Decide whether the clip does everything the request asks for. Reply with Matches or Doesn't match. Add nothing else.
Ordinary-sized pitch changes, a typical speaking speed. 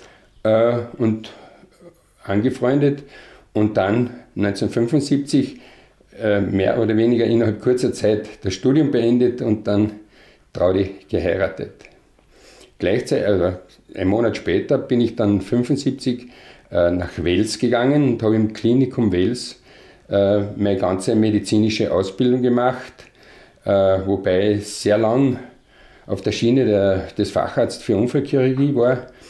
Doesn't match